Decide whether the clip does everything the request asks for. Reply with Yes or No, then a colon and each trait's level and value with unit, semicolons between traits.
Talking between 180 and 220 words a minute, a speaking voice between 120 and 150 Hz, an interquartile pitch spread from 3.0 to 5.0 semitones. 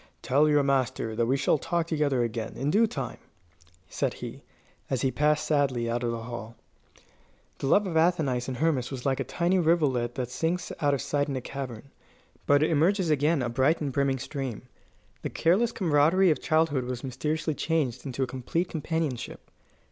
Yes: average, 185 wpm; medium, 140 Hz; average, 4.1 semitones